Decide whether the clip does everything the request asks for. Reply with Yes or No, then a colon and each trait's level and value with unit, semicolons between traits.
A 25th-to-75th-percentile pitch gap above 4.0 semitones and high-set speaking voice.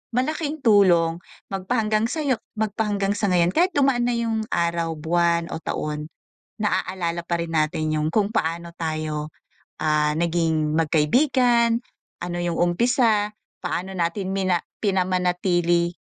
No: average, 4.6 semitones; medium, 180 Hz